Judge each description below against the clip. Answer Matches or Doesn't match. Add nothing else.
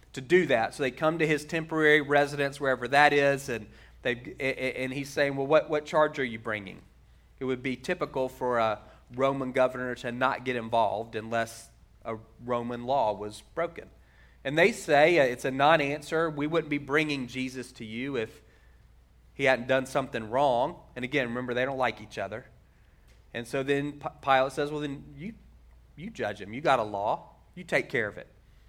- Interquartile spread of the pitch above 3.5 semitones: Doesn't match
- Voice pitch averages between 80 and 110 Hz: Doesn't match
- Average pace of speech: Matches